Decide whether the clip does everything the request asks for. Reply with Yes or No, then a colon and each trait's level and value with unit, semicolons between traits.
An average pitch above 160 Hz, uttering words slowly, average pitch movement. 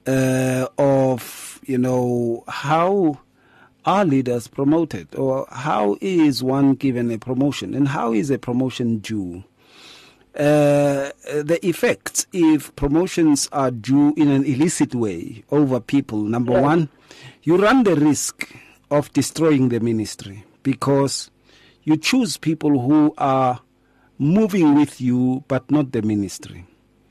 No: low, 135 Hz; slow, 125 wpm; average, 3.3 semitones